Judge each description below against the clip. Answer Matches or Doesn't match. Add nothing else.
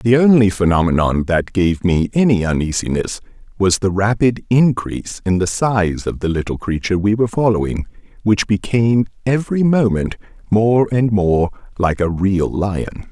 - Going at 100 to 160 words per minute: Matches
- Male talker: Matches